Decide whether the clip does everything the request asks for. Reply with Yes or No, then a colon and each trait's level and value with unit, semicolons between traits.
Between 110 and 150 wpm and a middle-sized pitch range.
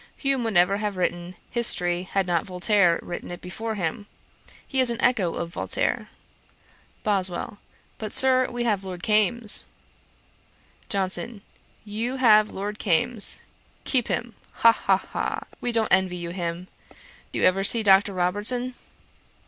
Yes: average, 145 wpm; average, 4.2 semitones